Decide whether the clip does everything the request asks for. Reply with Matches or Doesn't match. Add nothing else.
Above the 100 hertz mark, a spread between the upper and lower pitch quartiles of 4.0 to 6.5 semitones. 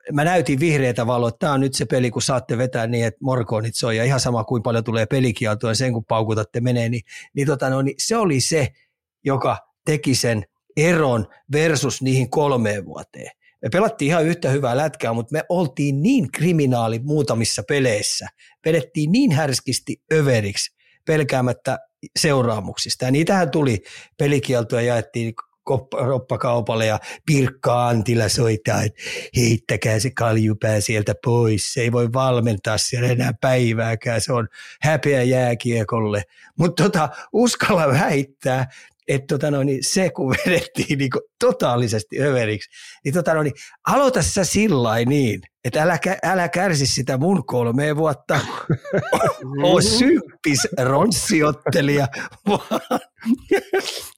Matches